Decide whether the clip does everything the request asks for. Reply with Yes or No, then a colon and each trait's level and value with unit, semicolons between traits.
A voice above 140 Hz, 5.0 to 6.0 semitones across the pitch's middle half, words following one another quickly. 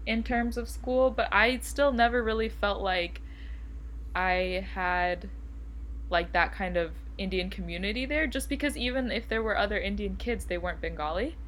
No: high, 190 Hz; wide, 5.5 semitones; average, 165 wpm